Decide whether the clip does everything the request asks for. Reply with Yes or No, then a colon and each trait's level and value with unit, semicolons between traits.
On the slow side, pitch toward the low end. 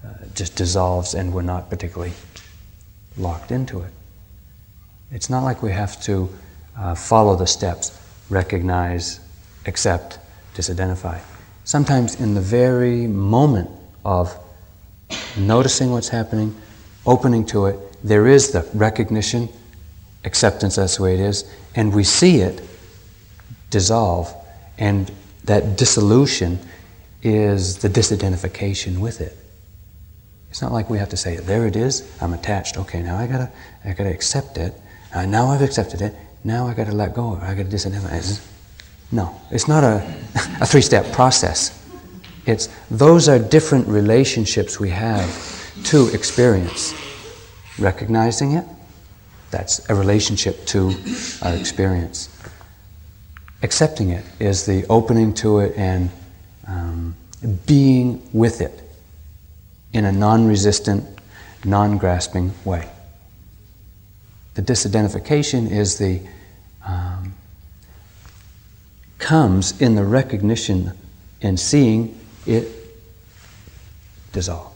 Yes: slow, 115 wpm; low, 100 Hz